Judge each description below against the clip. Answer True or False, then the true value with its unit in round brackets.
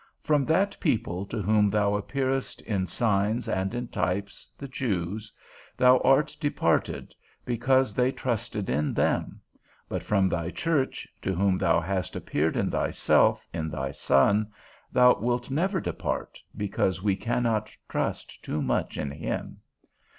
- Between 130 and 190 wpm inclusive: True (145 wpm)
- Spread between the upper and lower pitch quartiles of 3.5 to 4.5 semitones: False (5.1 semitones)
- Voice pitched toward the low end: True (105 Hz)